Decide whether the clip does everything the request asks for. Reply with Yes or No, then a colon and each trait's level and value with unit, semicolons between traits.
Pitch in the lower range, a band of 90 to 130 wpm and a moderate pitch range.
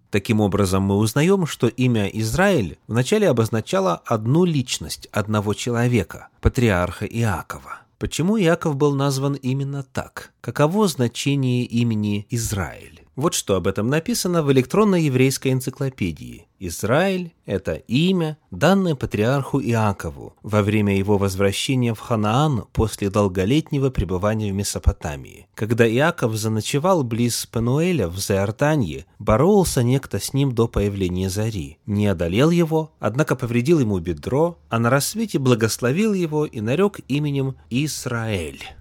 No: low, 120 Hz; average, 125 wpm; wide, 5.9 semitones